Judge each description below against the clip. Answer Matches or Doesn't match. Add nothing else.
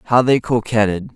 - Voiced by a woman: Doesn't match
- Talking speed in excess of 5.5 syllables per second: Doesn't match